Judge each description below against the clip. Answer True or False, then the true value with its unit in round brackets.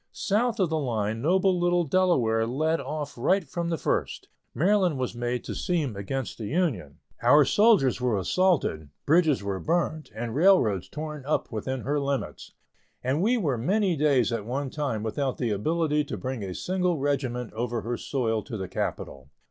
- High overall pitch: False (140 Hz)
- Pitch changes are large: True (6.5 semitones)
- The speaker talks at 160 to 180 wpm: True (175 wpm)